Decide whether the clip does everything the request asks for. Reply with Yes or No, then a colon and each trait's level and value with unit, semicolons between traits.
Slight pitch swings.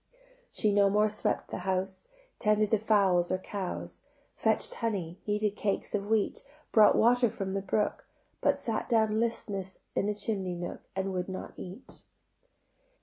Yes: narrow, 2.1 semitones